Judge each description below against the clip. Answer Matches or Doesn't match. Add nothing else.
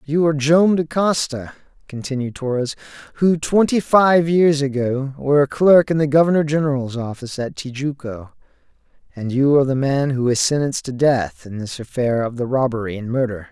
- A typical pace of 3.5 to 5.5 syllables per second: Matches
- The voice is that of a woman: Doesn't match